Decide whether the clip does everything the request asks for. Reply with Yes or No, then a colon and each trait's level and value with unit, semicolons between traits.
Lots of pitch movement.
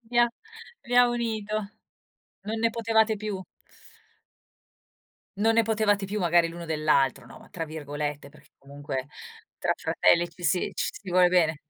Yes: wide, 5.7 semitones